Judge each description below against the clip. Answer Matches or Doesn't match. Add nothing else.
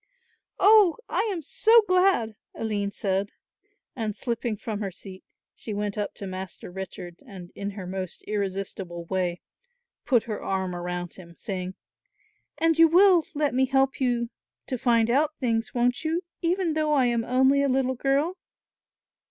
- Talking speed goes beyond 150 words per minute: Matches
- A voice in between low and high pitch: Doesn't match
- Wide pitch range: Matches